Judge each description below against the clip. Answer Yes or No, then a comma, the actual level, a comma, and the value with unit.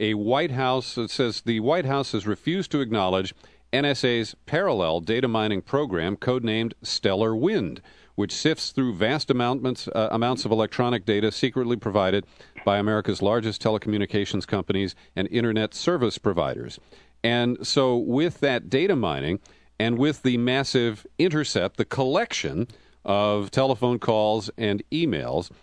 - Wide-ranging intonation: No, average, 3.4 semitones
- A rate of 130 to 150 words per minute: Yes, slow, 135 wpm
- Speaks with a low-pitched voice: Yes, low, 115 Hz